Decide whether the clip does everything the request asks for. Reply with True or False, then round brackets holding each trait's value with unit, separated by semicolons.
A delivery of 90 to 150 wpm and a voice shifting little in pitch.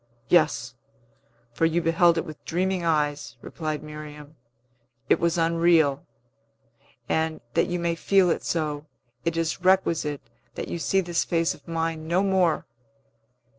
True (140 wpm; 2.1 semitones)